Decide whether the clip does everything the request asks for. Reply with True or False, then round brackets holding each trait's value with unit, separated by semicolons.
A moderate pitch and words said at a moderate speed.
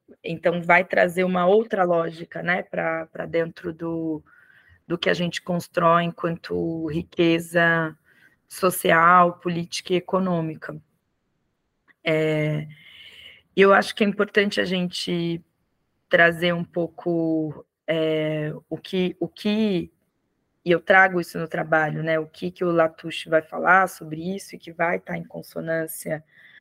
True (170 Hz; 135 wpm)